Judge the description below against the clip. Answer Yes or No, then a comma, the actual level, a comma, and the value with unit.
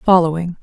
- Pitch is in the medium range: Yes, medium, 170 Hz